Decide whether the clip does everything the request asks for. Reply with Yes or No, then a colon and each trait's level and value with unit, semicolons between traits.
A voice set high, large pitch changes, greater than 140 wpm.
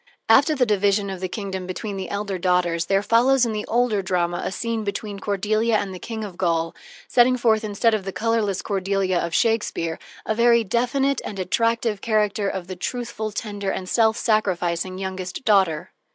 No: high, 205 Hz; average, 3.3 semitones; average, 180 wpm